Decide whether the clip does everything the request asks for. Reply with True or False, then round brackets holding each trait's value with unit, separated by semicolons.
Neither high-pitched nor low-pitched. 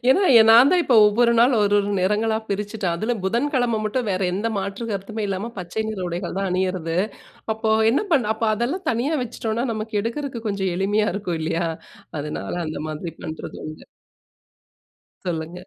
False (210 Hz)